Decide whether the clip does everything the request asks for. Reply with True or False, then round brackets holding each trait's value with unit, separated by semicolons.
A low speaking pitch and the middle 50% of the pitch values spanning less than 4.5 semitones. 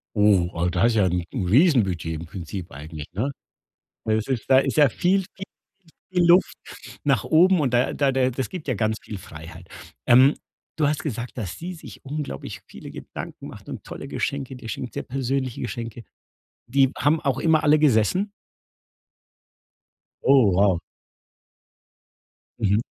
False (125 Hz; 6.5 semitones)